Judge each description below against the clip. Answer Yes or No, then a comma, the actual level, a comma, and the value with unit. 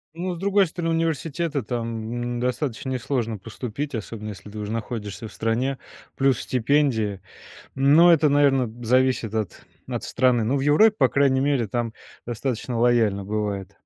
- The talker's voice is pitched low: Yes, low, 125 Hz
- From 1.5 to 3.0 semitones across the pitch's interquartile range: No, average, 4.1 semitones